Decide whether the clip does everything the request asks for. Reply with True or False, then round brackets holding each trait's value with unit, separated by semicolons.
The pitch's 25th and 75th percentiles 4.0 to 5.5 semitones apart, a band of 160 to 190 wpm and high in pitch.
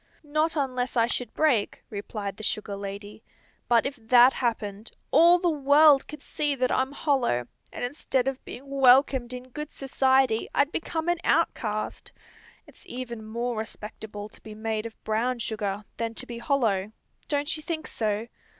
True (4.4 semitones; 165 wpm; 245 Hz)